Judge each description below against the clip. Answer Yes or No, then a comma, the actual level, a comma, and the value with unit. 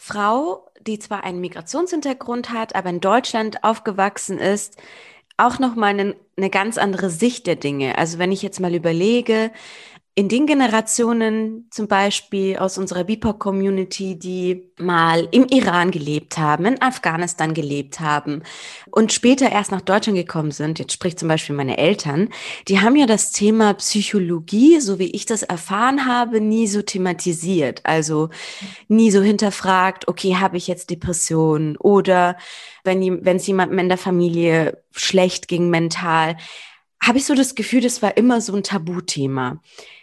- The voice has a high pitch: Yes, high, 195 Hz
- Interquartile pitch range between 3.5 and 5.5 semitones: Yes, average, 3.9 semitones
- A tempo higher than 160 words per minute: No, average, 155 wpm